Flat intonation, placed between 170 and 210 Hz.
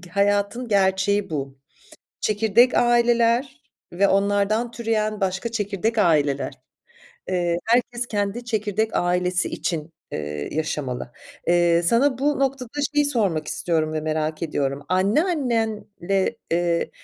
No: wide, 5.4 semitones; high, 200 Hz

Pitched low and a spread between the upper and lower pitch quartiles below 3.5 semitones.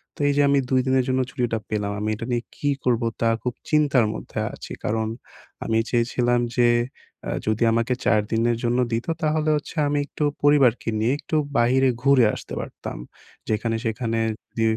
Yes: low, 120 Hz; average, 2.8 semitones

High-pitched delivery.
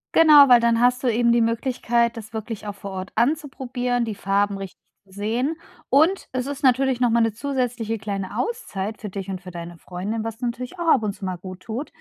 Yes: high, 230 Hz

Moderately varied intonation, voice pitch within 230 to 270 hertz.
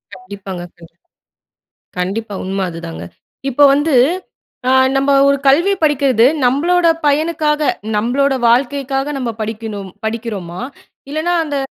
No: wide, 6.2 semitones; very high, 255 Hz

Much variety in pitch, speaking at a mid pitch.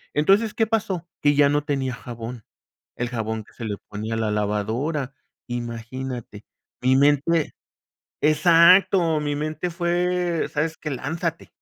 Yes: wide, 5.8 semitones; medium, 145 Hz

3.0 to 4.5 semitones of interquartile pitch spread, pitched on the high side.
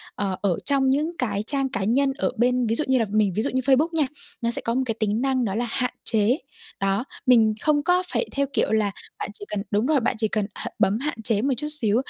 Yes: average, 4.2 semitones; high, 240 Hz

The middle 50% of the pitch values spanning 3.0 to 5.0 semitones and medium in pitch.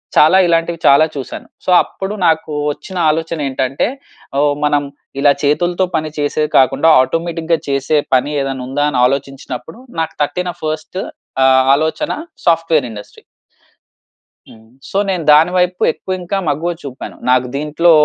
Yes: average, 3.4 semitones; medium, 155 Hz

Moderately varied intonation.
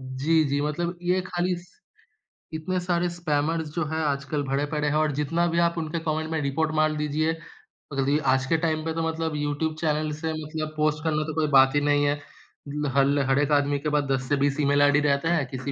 No: narrow, 2.0 semitones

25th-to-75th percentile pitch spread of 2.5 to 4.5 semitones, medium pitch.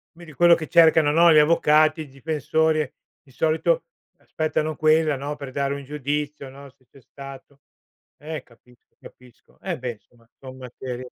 Yes: average, 2.9 semitones; medium, 145 Hz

